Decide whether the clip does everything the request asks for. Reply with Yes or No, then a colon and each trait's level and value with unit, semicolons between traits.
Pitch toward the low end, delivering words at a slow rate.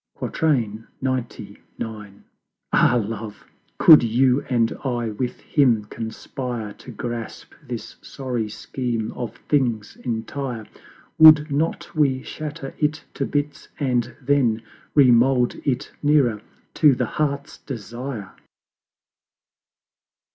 Yes: low, 125 Hz; slow, 105 wpm